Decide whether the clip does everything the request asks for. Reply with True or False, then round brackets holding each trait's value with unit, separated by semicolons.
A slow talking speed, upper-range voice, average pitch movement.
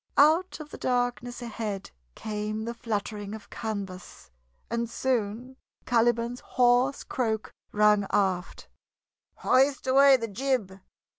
True (115 wpm; 235 Hz; 3.4 semitones)